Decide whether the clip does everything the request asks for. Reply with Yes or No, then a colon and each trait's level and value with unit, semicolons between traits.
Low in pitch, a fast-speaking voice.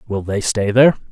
Yes: low, 110 Hz; fast, 215 wpm